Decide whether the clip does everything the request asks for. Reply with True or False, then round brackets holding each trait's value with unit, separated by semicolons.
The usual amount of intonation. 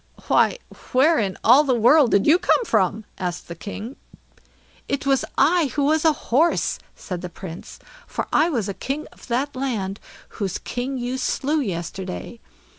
False (6.7 semitones)